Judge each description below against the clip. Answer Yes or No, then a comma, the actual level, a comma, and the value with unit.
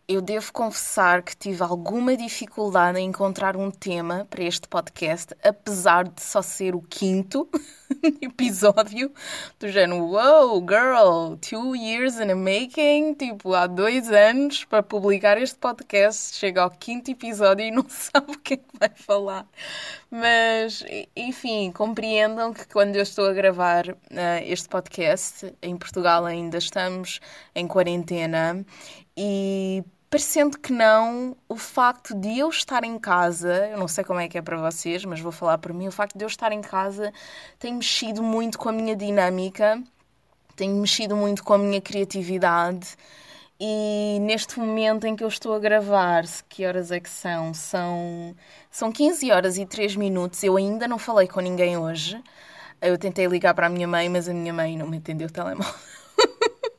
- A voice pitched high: Yes, high, 205 Hz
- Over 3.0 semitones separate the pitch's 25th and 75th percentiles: Yes, average, 4.3 semitones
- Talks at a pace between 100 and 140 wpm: No, average, 170 wpm